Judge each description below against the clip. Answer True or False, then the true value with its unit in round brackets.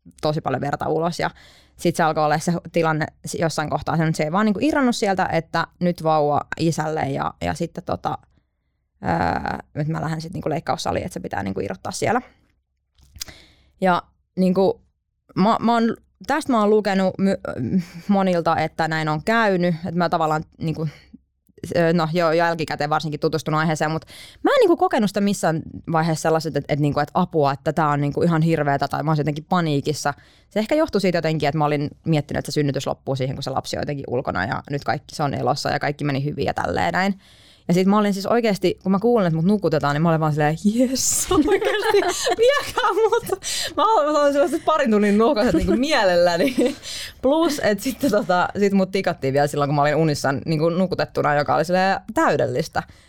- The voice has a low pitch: False (165 Hz)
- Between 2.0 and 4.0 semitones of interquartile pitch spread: False (5.3 semitones)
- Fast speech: True (195 wpm)